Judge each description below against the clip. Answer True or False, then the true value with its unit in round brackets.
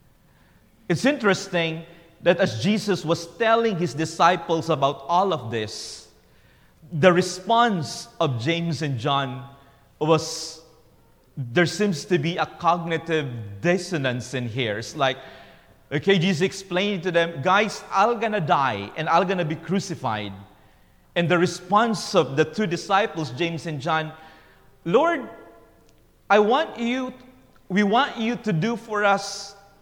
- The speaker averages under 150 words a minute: True (135 wpm)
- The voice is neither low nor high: True (170 Hz)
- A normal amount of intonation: True (4.4 semitones)